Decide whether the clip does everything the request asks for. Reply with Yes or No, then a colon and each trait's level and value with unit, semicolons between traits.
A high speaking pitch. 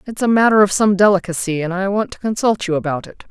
Yes: high, 195 Hz